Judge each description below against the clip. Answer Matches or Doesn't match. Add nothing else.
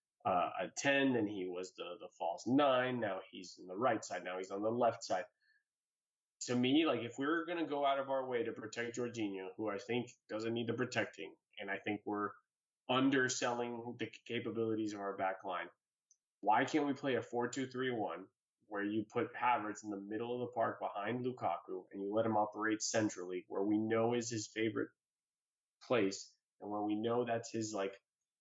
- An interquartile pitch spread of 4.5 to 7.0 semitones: Doesn't match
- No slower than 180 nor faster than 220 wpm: Matches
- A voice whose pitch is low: Matches